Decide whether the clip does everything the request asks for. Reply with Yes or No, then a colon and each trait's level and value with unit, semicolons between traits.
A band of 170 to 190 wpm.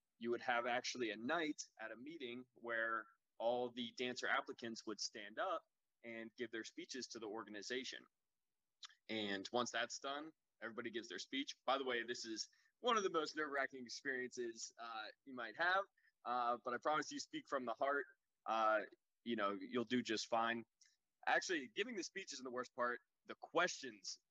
Yes: average, 180 wpm